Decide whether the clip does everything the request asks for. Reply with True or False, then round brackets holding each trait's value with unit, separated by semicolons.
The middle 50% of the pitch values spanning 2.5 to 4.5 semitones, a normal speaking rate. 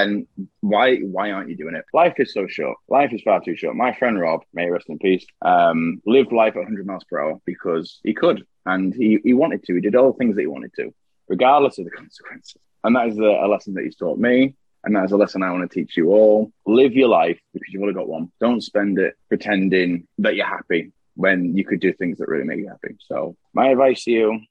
False (2.8 semitones; 255 wpm)